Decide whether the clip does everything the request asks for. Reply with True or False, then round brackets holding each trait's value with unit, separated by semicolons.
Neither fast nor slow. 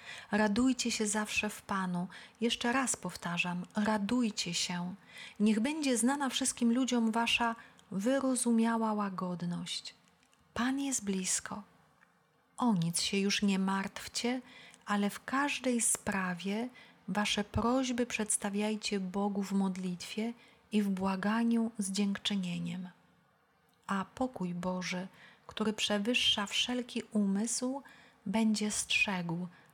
False (105 wpm)